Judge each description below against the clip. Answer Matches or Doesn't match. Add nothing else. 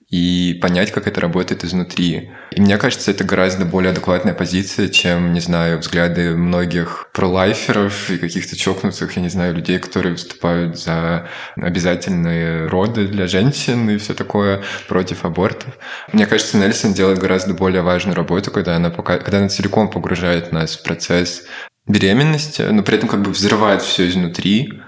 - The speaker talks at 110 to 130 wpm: Doesn't match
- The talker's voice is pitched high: Doesn't match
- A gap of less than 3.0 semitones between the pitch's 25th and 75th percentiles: Matches